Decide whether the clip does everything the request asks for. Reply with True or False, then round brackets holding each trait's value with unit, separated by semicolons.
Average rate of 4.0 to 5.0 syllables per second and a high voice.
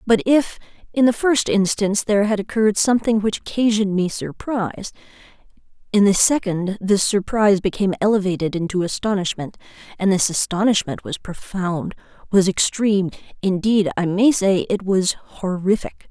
False (5.2 syllables/s; 200 Hz)